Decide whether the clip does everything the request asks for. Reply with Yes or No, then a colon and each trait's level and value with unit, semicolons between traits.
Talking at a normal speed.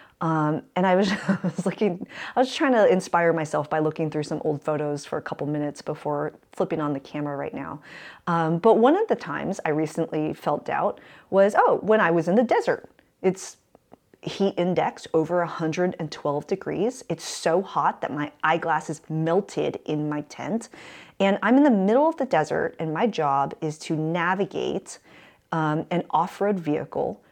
Yes: average, 180 wpm